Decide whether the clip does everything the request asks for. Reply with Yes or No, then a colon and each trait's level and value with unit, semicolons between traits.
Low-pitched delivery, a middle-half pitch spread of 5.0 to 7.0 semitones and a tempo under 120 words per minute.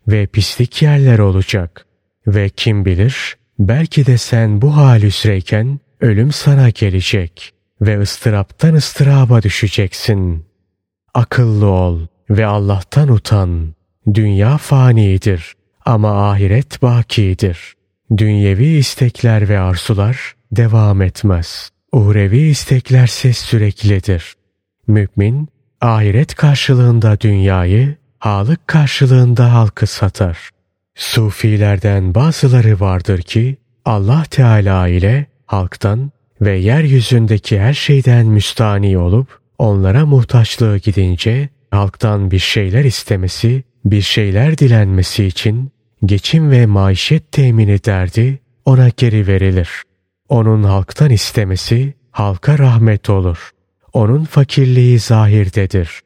No: low, 110 Hz; average, 4.1 semitones; slow, 95 wpm